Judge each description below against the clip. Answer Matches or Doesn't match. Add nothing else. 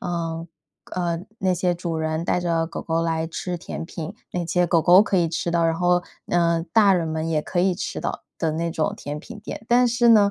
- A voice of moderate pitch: Matches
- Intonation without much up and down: Matches